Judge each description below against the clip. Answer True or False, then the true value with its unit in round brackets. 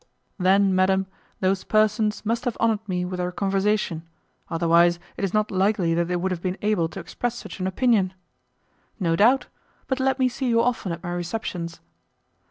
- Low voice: False (190 Hz)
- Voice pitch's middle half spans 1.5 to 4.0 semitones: True (3.5 semitones)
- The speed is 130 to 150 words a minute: False (180 wpm)